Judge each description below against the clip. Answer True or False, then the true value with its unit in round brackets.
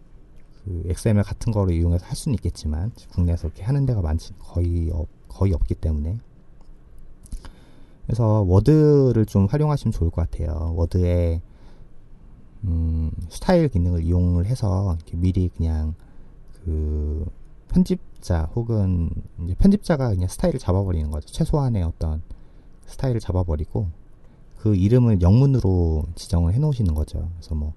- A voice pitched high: False (90 Hz)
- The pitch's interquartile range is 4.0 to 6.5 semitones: True (5.1 semitones)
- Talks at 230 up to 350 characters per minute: True (310 characters per minute)